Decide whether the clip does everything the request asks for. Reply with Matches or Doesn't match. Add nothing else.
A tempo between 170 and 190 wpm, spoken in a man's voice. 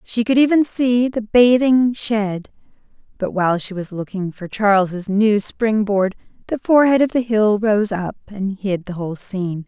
Doesn't match